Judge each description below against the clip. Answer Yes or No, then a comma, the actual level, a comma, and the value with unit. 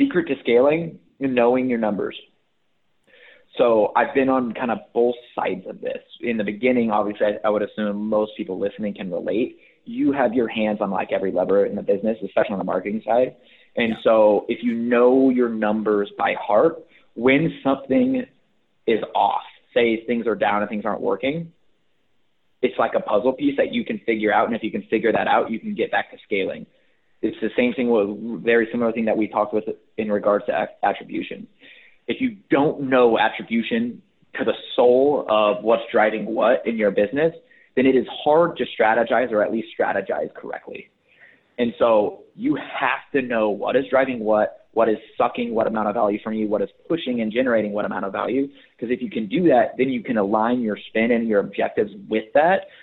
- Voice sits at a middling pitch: No, low, 120 Hz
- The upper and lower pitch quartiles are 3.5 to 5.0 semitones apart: Yes, average, 4.2 semitones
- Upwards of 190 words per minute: Yes, average, 200 wpm